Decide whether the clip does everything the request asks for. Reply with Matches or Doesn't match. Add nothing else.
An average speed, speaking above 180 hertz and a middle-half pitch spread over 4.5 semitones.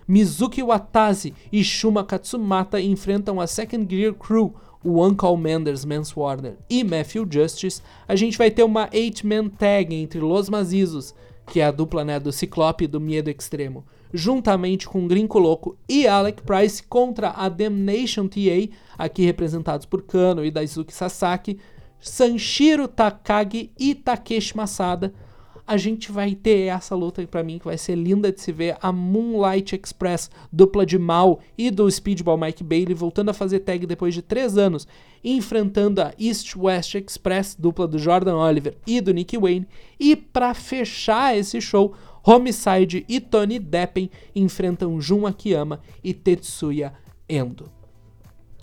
Doesn't match